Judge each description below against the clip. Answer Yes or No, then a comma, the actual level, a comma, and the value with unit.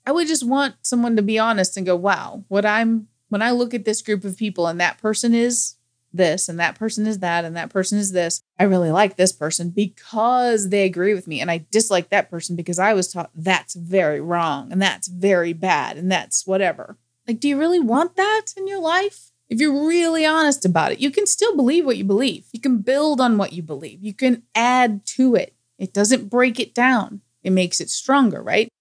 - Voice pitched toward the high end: Yes, high, 210 Hz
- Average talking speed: No, fast, 225 wpm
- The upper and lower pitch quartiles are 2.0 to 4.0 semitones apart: No, average, 5.2 semitones